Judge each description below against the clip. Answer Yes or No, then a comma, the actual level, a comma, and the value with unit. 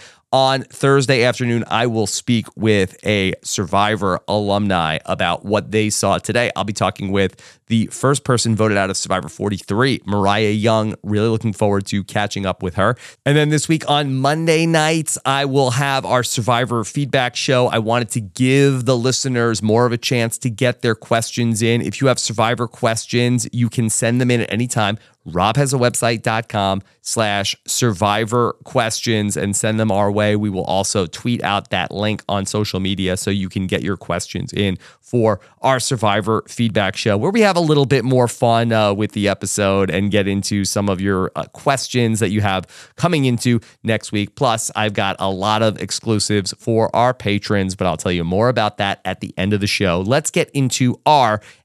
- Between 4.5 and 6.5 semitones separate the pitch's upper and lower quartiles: No, average, 3.7 semitones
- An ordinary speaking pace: Yes, average, 195 wpm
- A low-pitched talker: Yes, low, 110 Hz